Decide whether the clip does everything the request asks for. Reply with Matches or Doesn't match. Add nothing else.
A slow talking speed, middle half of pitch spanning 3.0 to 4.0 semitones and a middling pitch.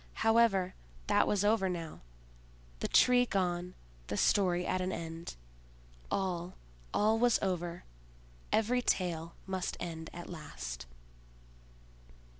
Matches